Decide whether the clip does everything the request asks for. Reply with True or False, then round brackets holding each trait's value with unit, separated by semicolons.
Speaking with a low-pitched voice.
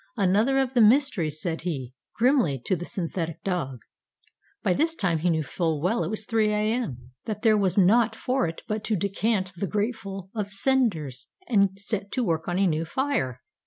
False (195 Hz)